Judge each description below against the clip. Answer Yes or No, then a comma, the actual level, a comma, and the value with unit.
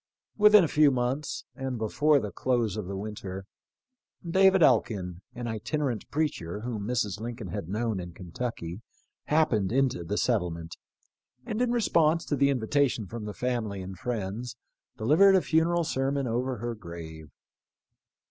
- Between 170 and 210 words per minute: No, average, 145 wpm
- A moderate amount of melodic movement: No, wide, 6.1 semitones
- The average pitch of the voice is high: No, low, 120 Hz